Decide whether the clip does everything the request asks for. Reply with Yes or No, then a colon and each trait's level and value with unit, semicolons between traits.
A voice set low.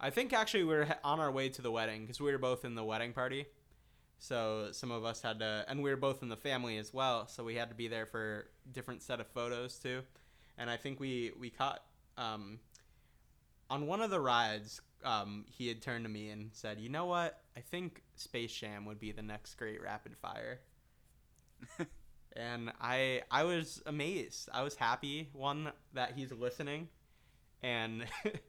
Yes: low, 120 Hz